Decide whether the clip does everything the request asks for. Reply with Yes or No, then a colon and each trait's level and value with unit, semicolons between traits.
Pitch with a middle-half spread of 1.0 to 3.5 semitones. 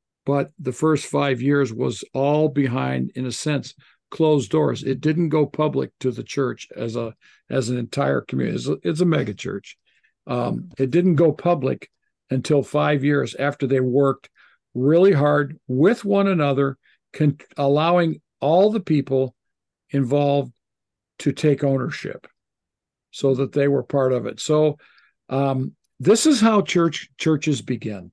Yes: narrow, 2.6 semitones